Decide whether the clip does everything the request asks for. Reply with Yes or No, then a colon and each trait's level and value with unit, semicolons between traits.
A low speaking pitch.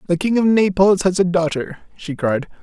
No: medium, 180 Hz